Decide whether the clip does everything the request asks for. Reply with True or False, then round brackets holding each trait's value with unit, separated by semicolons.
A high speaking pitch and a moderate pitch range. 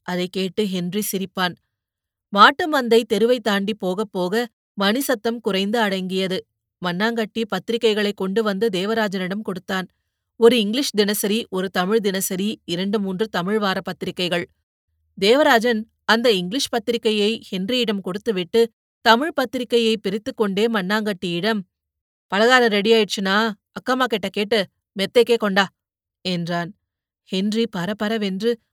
True (210 Hz; 3.3 semitones)